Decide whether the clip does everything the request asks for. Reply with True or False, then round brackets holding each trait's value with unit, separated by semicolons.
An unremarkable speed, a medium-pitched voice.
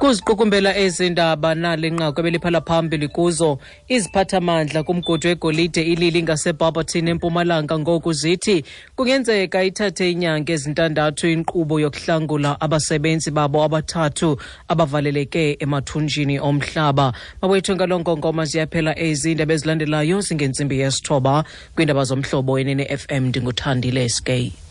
False (90 wpm; 160 Hz)